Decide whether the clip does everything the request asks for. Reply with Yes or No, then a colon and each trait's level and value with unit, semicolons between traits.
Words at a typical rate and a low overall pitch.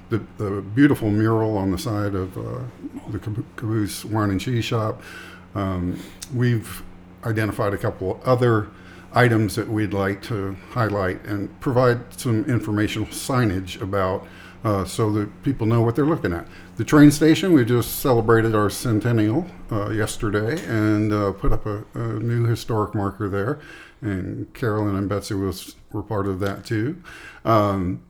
Yes: average, 160 wpm; low, 105 Hz